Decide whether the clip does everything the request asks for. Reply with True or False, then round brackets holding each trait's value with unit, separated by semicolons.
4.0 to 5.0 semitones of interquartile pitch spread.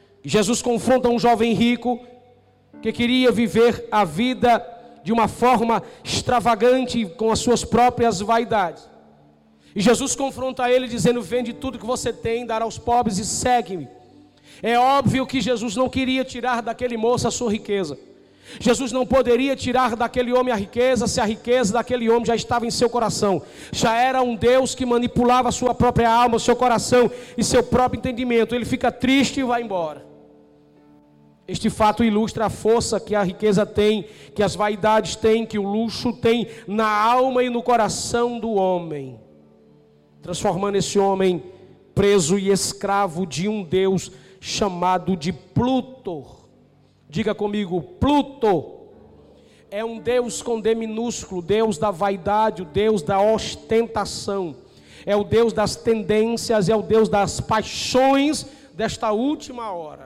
False (3.2 semitones)